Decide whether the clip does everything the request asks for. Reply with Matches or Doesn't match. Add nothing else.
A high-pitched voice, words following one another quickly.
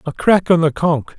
Doesn't match